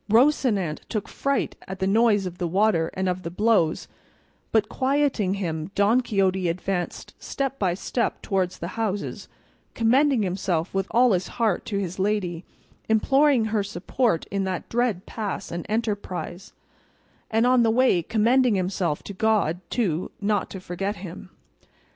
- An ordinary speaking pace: Yes, average, 155 wpm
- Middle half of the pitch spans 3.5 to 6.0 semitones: Yes, average, 3.9 semitones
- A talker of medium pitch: No, high, 200 Hz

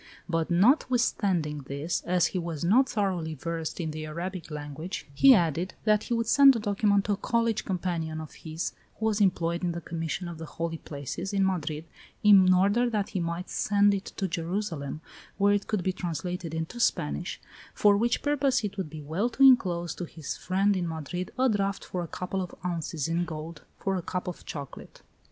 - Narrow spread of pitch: No, average, 3.8 semitones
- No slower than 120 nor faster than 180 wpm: No, average, 195 wpm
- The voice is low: No, medium, 180 Hz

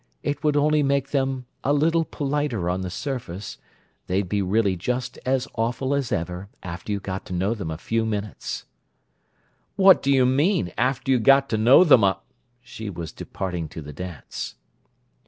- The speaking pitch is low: Yes, low, 115 Hz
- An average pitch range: No, wide, 6.7 semitones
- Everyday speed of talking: Yes, average, 175 wpm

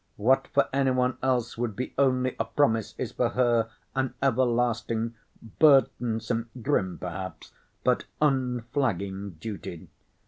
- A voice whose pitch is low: Yes, low, 120 Hz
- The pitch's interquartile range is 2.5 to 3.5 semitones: Yes, average, 2.8 semitones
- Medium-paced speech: No, slow, 125 wpm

